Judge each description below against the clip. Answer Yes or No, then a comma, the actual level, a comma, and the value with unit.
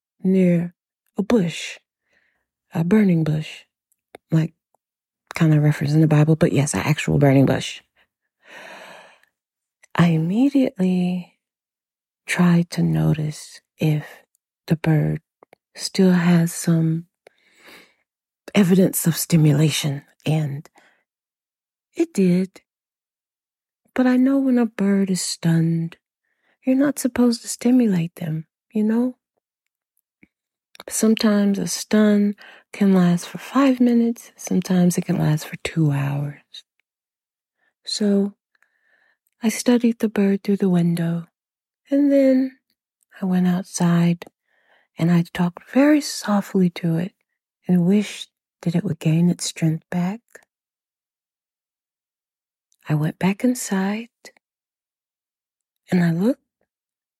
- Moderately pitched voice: Yes, medium, 180 Hz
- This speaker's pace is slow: Yes, slow, 110 wpm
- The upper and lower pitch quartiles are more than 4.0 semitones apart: Yes, average, 5.1 semitones